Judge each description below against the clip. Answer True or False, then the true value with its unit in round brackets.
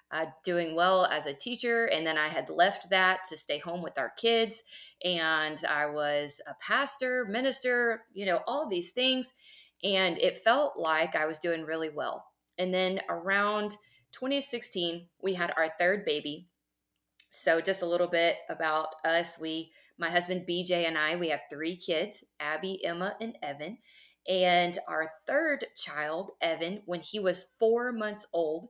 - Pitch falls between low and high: True (175 Hz)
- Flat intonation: False (4.6 semitones)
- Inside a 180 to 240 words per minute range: False (165 wpm)